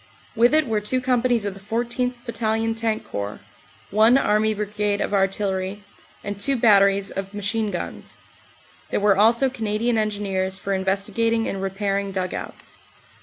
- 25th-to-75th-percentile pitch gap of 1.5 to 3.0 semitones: Yes, narrow, 2.6 semitones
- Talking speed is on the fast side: No, average, 155 wpm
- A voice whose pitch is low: No, high, 210 Hz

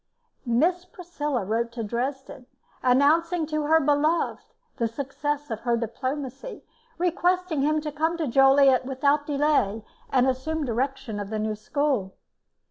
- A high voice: Yes, very high, 275 Hz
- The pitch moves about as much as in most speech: Yes, average, 4.0 semitones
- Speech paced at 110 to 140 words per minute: Yes, slow, 135 wpm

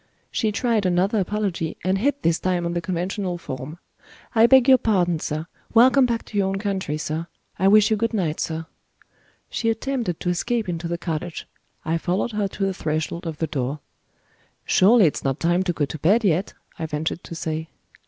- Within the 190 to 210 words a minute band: Yes, average, 195 wpm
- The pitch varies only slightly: No, average, 4.7 semitones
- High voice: No, medium, 180 Hz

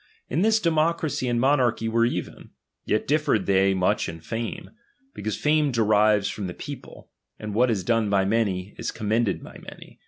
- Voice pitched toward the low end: Yes, low, 115 Hz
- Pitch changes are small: No, average, 4.3 semitones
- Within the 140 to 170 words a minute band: No, average, 180 wpm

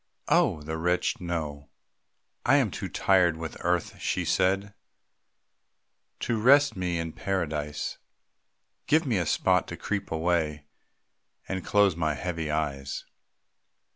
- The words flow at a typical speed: No, slow, 125 wpm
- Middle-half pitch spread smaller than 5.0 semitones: Yes, average, 3.6 semitones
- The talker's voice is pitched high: No, very low, 85 Hz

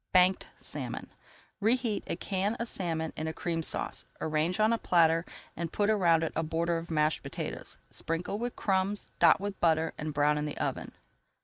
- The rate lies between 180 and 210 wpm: Yes, average, 185 wpm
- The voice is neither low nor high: Yes, medium, 170 Hz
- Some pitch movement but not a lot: Yes, average, 3.9 semitones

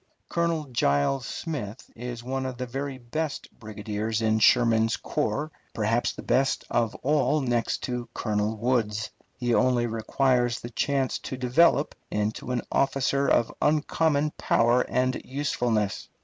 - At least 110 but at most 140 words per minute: Yes, slow, 135 wpm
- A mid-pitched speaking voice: No, low, 125 Hz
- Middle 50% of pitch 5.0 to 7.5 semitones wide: No, average, 3.4 semitones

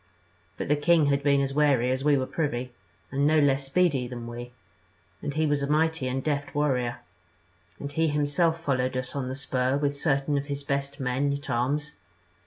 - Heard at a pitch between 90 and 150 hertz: Yes, medium, 140 Hz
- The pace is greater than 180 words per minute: Yes, average, 195 wpm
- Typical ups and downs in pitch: No, narrow, 2.2 semitones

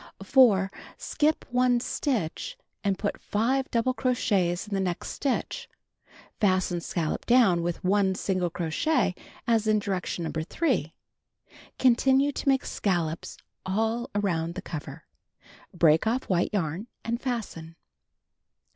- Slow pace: Yes, slow, 125 wpm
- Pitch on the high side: Yes, high, 200 Hz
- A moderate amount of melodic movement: No, wide, 6.0 semitones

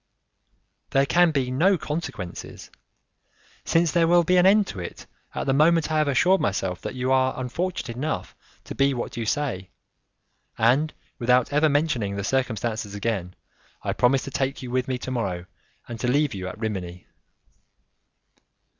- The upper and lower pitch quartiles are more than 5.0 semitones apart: Yes, wide, 5.6 semitones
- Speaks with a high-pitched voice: No, low, 130 Hz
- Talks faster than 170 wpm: No, average, 165 wpm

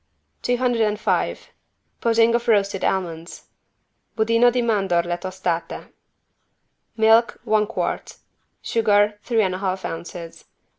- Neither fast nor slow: No, slow, 100 wpm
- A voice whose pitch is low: No, high, 210 Hz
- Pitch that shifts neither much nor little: Yes, average, 3.6 semitones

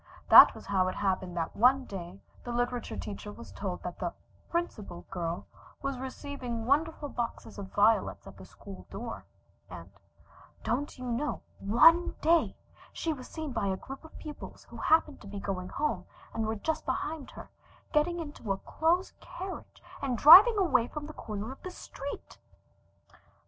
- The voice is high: Yes, very high, 255 Hz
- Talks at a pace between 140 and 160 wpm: No, average, 170 wpm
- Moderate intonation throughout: No, wide, 7.1 semitones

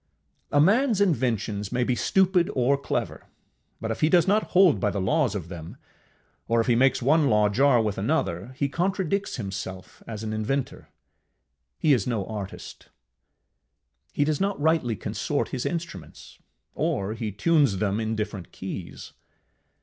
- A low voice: Yes, low, 120 Hz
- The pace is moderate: Yes, average, 155 wpm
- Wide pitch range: Yes, wide, 7.2 semitones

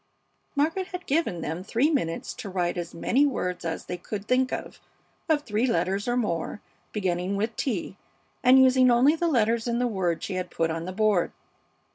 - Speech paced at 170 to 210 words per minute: Yes, average, 190 wpm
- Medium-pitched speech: No, high, 215 Hz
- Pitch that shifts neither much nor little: No, wide, 6.1 semitones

